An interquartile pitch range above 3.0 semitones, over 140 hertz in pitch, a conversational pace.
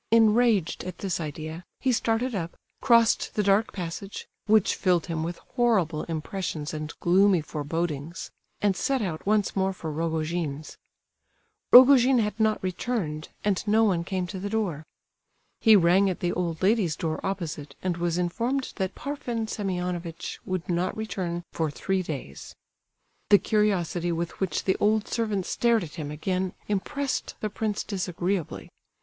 Yes: average, 4.2 semitones; medium, 185 Hz; average, 150 wpm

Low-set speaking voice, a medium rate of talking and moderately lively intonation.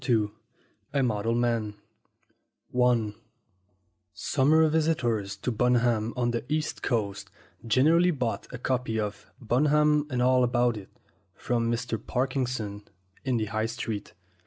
No: low, 120 Hz; slow, 120 wpm; average, 3.0 semitones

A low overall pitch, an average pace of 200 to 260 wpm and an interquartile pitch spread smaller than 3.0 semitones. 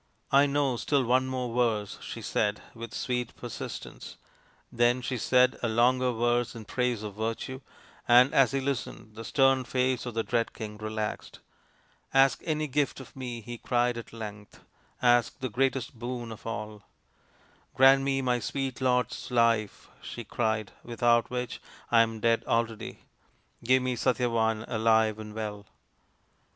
No: low, 120 Hz; average, 165 wpm; narrow, 2.4 semitones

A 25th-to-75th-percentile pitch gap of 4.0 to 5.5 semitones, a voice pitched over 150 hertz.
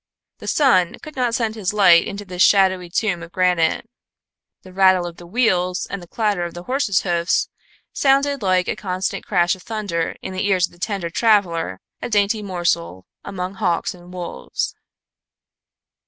No: average, 3.0 semitones; medium, 185 Hz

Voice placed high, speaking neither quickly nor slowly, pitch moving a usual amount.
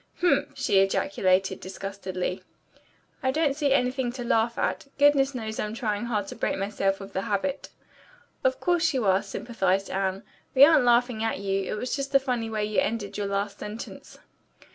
Yes: high, 220 Hz; average, 175 wpm; average, 4.9 semitones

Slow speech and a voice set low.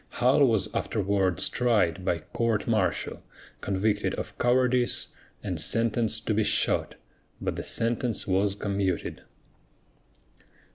Yes: slow, 110 wpm; low, 110 Hz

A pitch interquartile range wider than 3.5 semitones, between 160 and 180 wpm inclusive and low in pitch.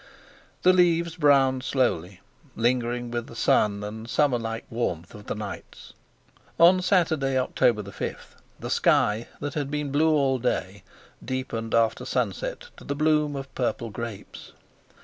No: average, 4.7 semitones; average, 145 wpm; low, 130 Hz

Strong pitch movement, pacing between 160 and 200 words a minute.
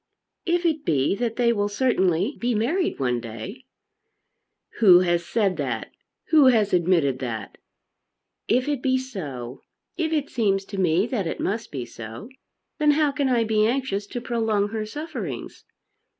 Yes: wide, 7.0 semitones; average, 165 wpm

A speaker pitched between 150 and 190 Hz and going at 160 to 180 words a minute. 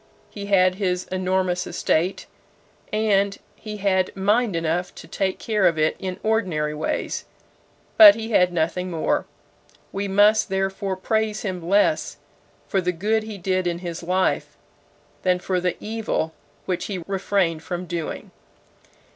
No: medium, 185 Hz; average, 145 wpm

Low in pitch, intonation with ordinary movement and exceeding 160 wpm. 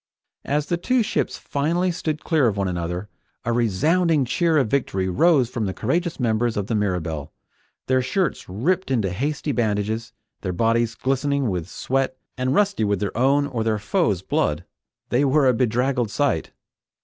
No: low, 125 Hz; wide, 6.0 semitones; average, 170 wpm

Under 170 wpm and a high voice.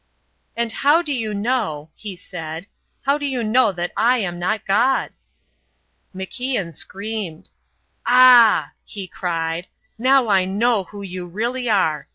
Yes: average, 140 wpm; high, 210 Hz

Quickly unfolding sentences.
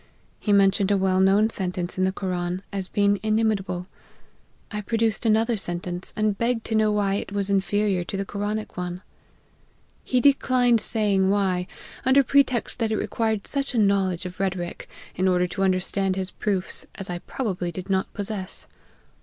No: average, 170 wpm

